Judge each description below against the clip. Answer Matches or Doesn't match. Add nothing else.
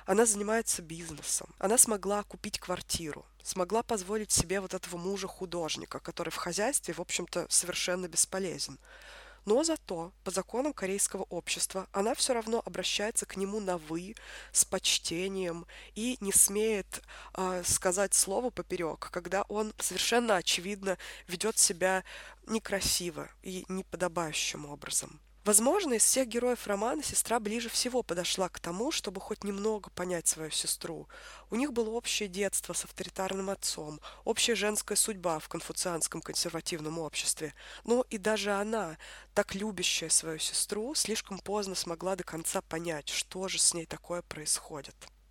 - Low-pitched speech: Doesn't match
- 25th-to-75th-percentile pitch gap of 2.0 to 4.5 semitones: Matches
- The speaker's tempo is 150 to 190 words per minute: Doesn't match